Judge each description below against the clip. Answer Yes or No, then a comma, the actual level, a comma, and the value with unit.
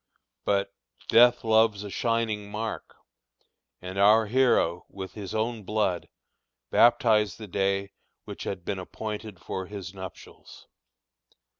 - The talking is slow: Yes, slow, 120 wpm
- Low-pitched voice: Yes, low, 105 Hz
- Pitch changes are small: Yes, narrow, 2.3 semitones